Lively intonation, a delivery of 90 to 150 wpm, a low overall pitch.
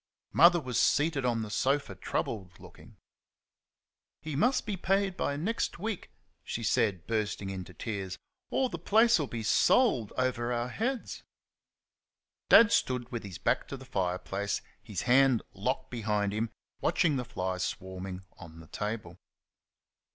Yes: wide, 7.3 semitones; average, 145 wpm; low, 120 Hz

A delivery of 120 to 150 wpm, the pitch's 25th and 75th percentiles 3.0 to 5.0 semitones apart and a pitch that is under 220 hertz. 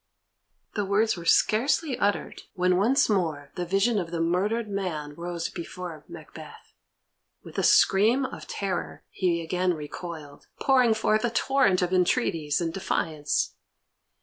Yes: average, 140 wpm; average, 4.3 semitones; medium, 185 Hz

